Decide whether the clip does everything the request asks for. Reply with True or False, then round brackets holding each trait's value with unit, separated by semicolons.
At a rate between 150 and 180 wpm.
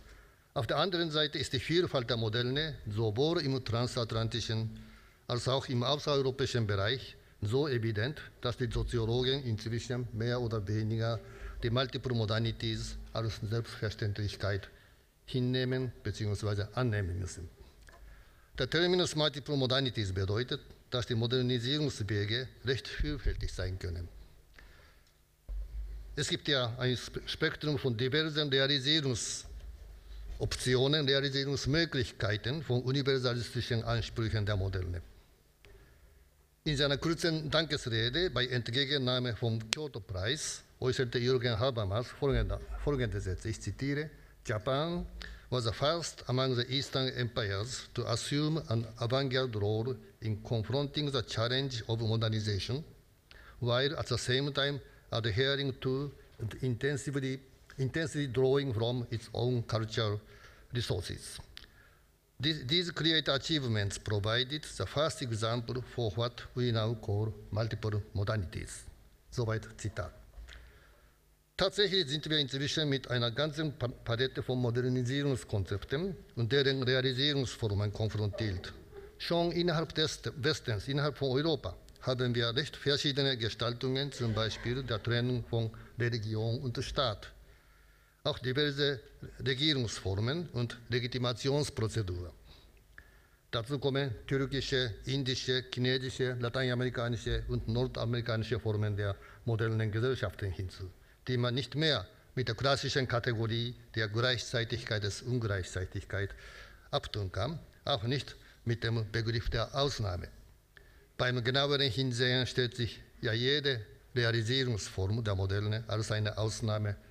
True (155 wpm)